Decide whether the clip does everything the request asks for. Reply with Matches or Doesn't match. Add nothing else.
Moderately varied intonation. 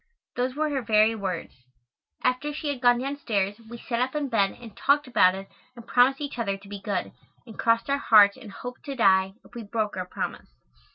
Matches